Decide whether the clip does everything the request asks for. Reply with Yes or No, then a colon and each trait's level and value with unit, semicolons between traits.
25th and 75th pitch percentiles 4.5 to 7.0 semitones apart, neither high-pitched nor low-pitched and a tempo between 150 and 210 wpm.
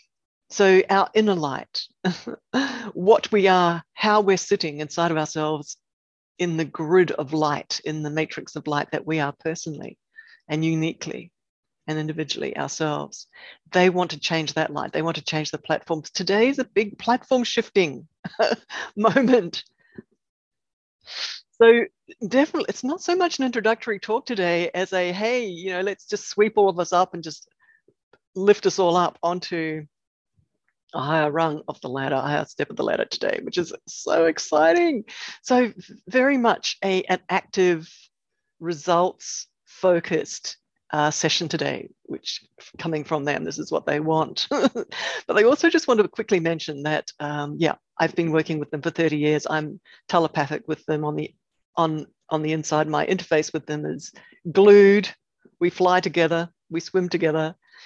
Yes: average, 5.0 semitones; medium, 175 Hz; average, 165 wpm